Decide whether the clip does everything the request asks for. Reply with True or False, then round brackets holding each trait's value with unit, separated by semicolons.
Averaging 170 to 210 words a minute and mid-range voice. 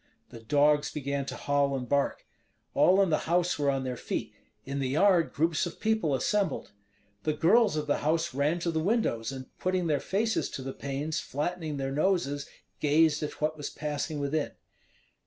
True (185 wpm; 150 Hz)